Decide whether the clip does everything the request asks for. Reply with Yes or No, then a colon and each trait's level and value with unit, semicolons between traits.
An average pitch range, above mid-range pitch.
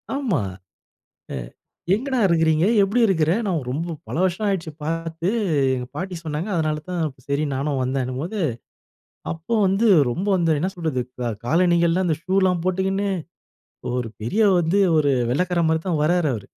No: average, 3.5 semitones; medium, 170 Hz